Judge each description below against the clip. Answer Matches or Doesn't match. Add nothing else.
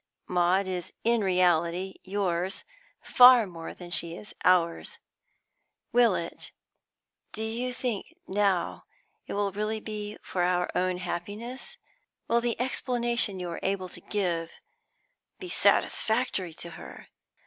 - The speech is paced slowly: Matches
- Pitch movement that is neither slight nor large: Matches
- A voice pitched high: Matches